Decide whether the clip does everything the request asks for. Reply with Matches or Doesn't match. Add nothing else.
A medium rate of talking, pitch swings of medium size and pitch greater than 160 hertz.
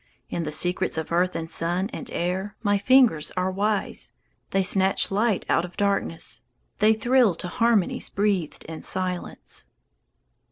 Matches